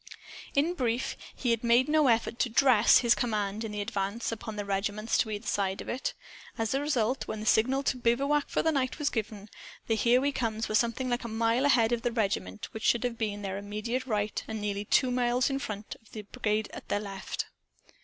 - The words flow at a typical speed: No, fast, 225 wpm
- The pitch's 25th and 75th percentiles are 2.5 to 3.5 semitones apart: Yes, average, 3.1 semitones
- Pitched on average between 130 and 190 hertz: No, high, 230 Hz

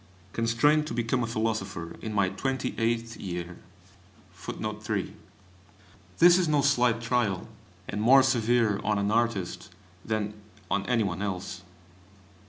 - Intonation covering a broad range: No, average, 3.4 semitones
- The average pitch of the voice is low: Yes, low, 110 Hz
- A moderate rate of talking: No, slow, 125 wpm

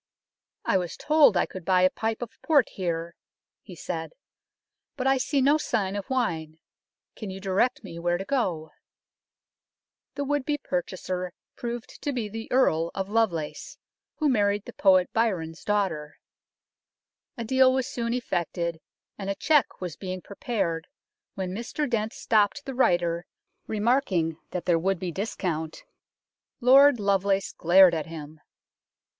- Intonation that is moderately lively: No, wide, 5.8 semitones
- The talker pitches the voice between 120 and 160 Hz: No, high, 195 Hz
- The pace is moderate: Yes, average, 155 wpm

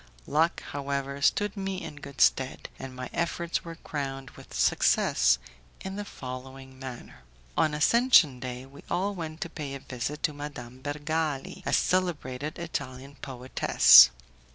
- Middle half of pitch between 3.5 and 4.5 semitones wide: Yes, average, 3.9 semitones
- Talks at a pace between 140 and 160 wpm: Yes, average, 145 wpm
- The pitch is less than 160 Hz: Yes, medium, 140 Hz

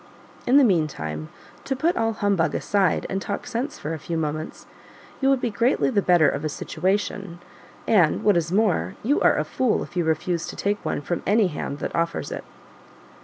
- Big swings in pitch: Yes, wide, 5.7 semitones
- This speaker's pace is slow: No, average, 200 wpm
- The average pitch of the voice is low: No, high, 190 Hz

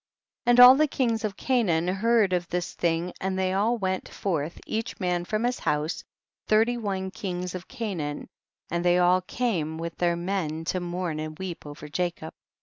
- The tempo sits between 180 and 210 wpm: Yes, average, 185 wpm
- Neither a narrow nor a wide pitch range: Yes, average, 4.0 semitones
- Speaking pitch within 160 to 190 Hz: Yes, medium, 185 Hz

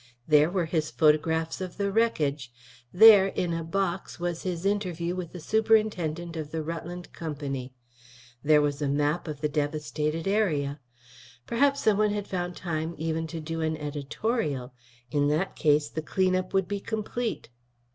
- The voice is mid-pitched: Yes, medium, 165 Hz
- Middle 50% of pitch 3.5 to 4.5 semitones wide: Yes, average, 4.1 semitones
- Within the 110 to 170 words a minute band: Yes, average, 160 wpm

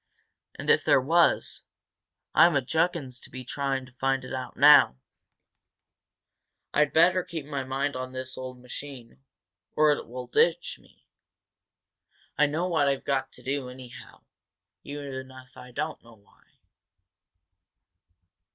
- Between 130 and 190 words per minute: Yes, slow, 135 wpm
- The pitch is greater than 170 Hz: No, low, 135 Hz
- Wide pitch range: No, narrow, 2.5 semitones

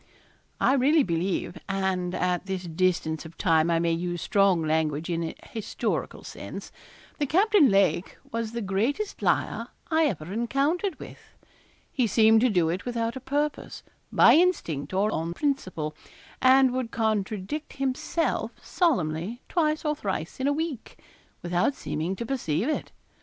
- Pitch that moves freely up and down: Yes, wide, 7.8 semitones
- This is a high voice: Yes, high, 210 Hz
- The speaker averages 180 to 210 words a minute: No, average, 150 wpm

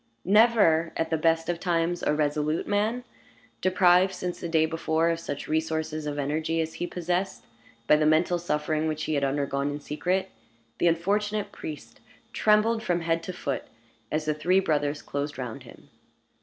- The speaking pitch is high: No, medium, 165 Hz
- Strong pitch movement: No, average, 2.8 semitones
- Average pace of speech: Yes, average, 170 wpm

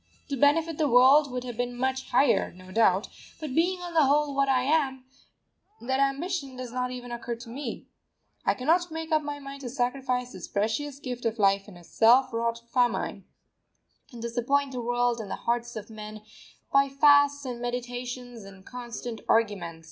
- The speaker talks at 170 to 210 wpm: Yes, average, 185 wpm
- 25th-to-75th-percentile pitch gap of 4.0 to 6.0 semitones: No, average, 3.1 semitones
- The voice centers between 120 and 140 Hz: No, very high, 250 Hz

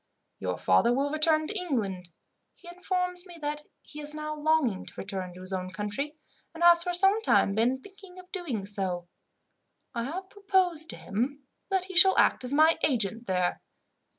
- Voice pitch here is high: Yes, very high, 300 Hz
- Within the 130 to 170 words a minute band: No, average, 180 wpm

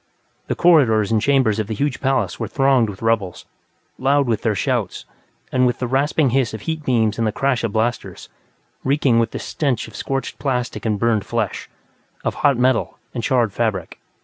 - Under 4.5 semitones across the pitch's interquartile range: Yes, average, 3.5 semitones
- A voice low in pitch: Yes, low, 120 Hz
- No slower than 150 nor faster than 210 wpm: Yes, average, 190 wpm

